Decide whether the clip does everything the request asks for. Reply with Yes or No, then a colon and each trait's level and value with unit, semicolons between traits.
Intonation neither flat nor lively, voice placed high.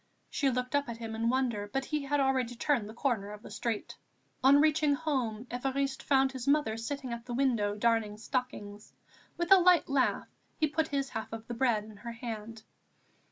Yes: average, 3.6 semitones; very high, 250 Hz